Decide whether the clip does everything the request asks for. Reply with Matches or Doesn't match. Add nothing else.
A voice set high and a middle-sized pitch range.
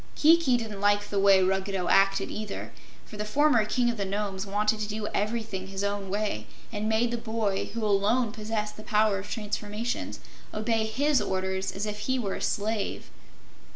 Doesn't match